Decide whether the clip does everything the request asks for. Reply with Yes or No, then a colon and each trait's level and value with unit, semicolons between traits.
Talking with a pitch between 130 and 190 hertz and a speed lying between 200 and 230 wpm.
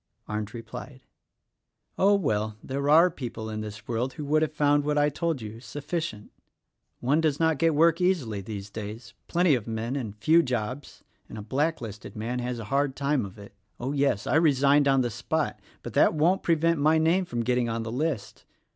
Yes: low, 135 Hz; fast, 205 wpm